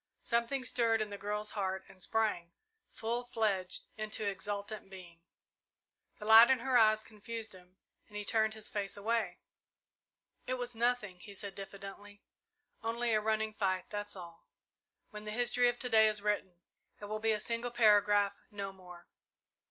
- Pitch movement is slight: Yes, narrow, 2.3 semitones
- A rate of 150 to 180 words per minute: Yes, average, 165 wpm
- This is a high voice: Yes, high, 210 Hz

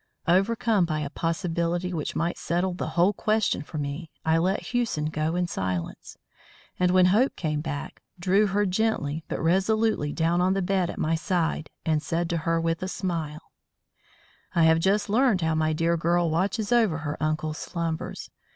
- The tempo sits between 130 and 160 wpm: No, average, 180 wpm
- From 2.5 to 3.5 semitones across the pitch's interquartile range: Yes, average, 3.1 semitones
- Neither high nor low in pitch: Yes, medium, 170 Hz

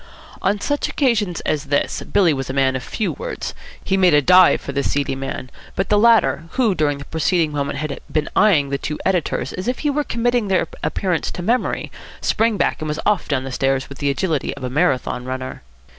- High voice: No, medium, 160 Hz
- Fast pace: Yes, fast, 220 wpm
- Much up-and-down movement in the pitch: Yes, wide, 6.7 semitones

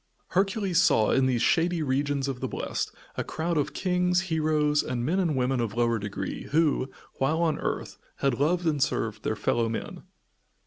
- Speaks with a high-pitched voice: No, medium, 150 Hz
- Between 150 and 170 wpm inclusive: No, average, 180 wpm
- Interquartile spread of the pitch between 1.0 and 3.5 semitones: No, average, 5.0 semitones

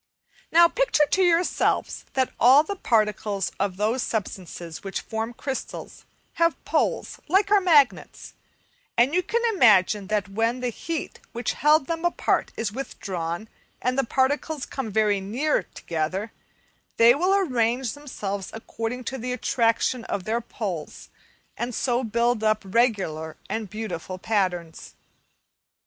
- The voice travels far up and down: No, average, 4.9 semitones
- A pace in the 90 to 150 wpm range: Yes, slow, 135 wpm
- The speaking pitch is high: Yes, high, 230 Hz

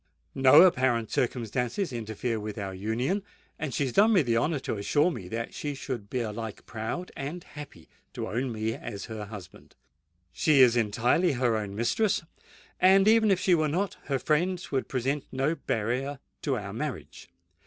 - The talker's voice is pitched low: Yes, low, 130 Hz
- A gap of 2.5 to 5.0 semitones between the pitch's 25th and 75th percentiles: No, wide, 5.6 semitones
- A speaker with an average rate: Yes, average, 175 wpm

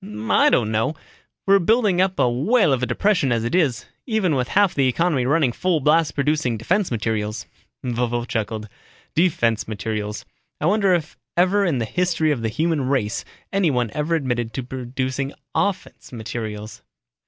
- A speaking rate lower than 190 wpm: Yes, average, 165 wpm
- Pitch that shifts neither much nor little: No, wide, 6.9 semitones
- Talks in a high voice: No, low, 135 Hz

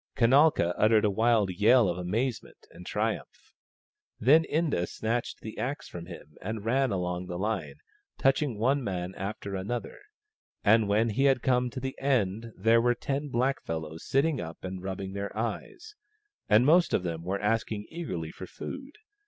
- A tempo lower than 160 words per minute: No, average, 165 wpm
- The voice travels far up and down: Yes, wide, 5.7 semitones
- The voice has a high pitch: No, low, 110 Hz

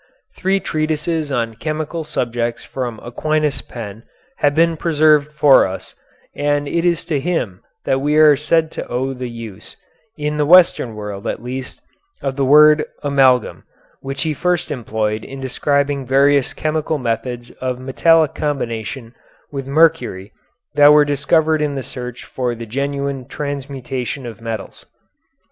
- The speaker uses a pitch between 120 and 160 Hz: Yes, medium, 140 Hz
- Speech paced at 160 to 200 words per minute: No, average, 145 wpm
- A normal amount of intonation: Yes, average, 3.7 semitones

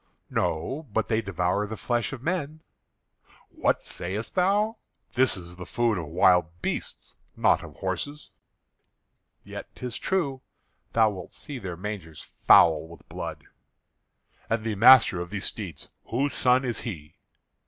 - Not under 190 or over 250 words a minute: No, average, 145 wpm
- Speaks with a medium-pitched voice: No, low, 110 Hz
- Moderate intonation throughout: No, wide, 6.7 semitones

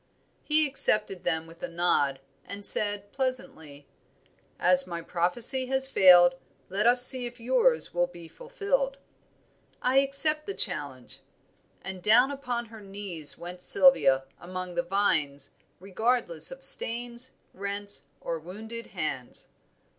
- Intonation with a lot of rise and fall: Yes, wide, 6.6 semitones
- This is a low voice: No, high, 205 Hz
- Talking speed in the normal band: No, slow, 130 wpm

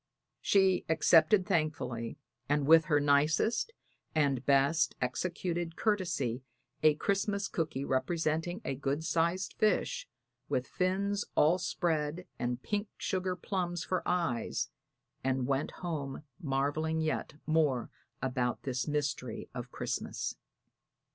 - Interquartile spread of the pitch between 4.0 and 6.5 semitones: Yes, average, 4.7 semitones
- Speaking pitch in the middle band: Yes, medium, 160 Hz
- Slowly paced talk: Yes, slow, 115 wpm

